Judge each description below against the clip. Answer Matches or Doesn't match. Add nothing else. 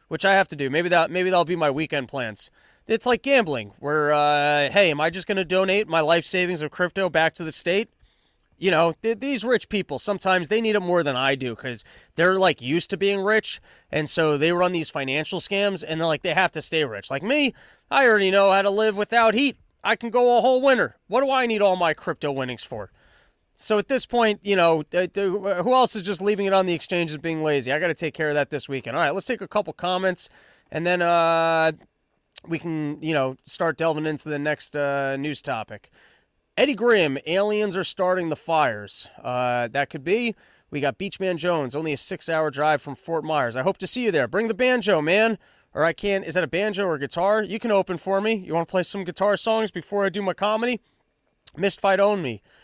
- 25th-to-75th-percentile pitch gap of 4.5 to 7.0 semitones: Matches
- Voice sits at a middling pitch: Matches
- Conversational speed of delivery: Doesn't match